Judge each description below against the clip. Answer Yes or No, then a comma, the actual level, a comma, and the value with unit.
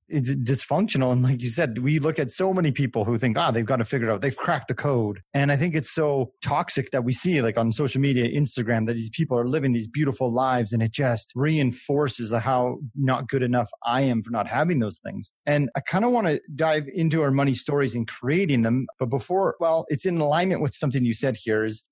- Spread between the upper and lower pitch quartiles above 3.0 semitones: Yes, average, 3.6 semitones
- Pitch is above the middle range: No, low, 135 Hz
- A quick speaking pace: Yes, fast, 245 wpm